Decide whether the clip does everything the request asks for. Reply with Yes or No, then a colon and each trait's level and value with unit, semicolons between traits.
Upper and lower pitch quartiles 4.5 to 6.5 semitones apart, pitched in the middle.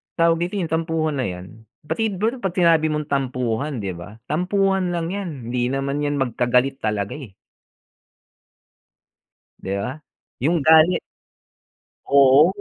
Yes: average, 5.2 semitones; medium, 145 Hz